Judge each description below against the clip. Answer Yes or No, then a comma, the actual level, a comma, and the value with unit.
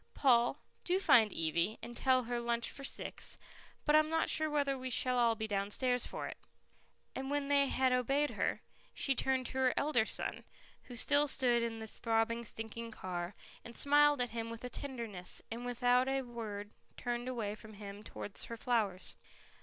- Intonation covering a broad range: No, average, 3.1 semitones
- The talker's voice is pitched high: Yes, high, 240 Hz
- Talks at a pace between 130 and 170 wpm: No, average, 180 wpm